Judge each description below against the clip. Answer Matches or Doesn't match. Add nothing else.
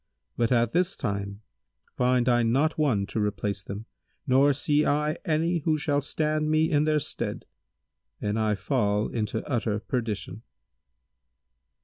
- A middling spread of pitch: Doesn't match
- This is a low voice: Matches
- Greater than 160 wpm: Doesn't match